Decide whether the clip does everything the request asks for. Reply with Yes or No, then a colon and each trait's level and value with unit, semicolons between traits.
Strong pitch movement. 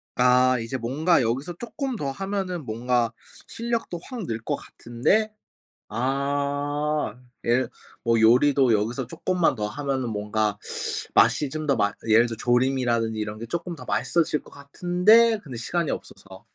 Yes: wide, 6.2 semitones